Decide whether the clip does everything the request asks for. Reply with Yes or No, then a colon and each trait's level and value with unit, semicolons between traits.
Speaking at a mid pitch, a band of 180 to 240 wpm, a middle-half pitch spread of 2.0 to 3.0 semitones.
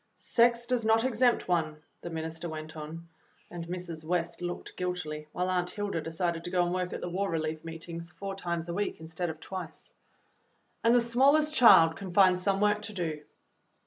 No: medium, 175 Hz; average, 195 wpm; average, 3.5 semitones